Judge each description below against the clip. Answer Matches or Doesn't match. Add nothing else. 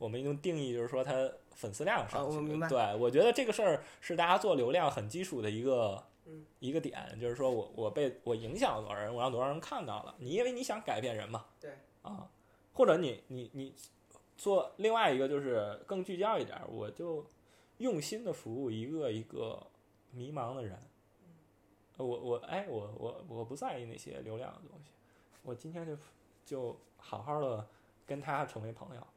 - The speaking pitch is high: Doesn't match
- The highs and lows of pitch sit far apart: Matches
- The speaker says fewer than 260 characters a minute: Doesn't match